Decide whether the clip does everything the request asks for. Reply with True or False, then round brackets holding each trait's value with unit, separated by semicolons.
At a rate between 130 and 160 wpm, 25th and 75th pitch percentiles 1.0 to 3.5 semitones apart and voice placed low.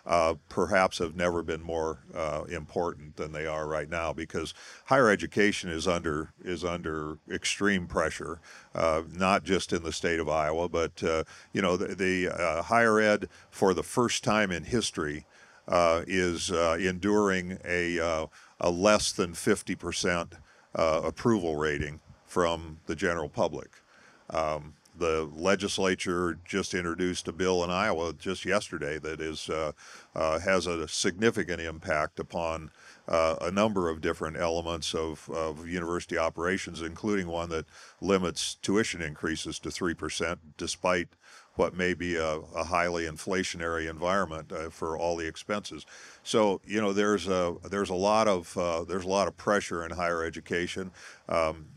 True (155 wpm; 2.6 semitones; 85 Hz)